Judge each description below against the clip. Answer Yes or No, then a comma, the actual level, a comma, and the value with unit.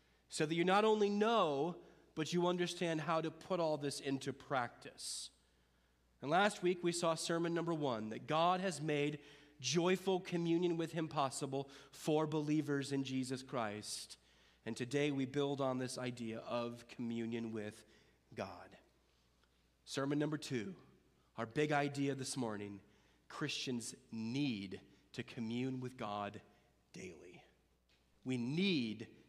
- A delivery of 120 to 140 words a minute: Yes, slow, 135 wpm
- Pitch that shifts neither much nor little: No, wide, 6.3 semitones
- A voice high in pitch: No, low, 135 Hz